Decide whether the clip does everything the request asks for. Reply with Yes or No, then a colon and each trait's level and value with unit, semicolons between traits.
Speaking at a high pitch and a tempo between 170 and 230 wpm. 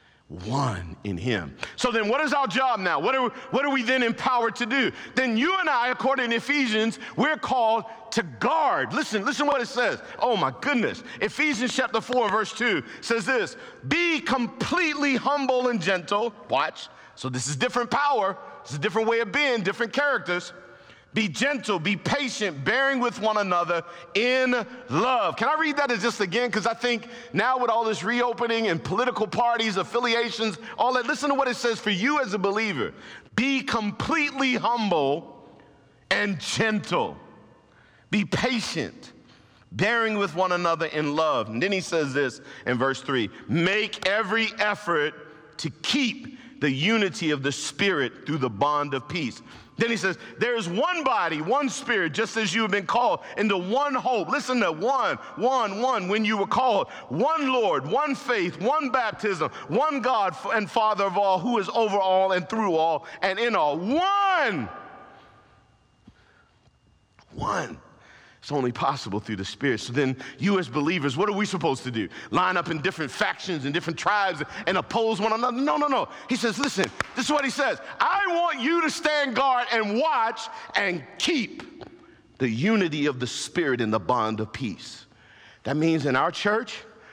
Yes: high, 225 Hz; average, 180 wpm